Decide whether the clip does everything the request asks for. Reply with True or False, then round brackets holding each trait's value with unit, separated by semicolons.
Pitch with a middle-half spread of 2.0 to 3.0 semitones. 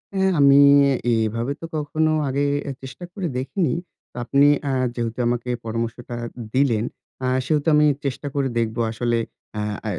False (3.7 semitones)